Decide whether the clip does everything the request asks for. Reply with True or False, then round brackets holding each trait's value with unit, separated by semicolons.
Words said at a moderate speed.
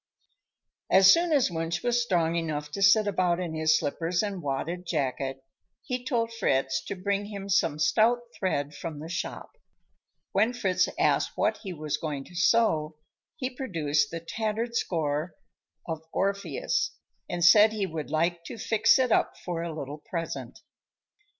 True (160 wpm)